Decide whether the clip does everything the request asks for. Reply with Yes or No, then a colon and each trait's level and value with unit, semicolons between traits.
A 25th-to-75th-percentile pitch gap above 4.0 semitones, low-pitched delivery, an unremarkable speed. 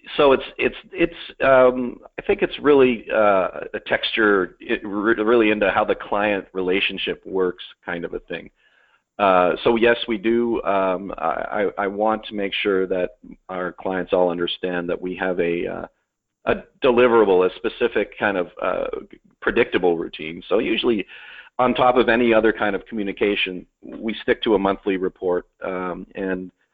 Yes: average, 5.1 semitones; low, 105 Hz; average, 165 wpm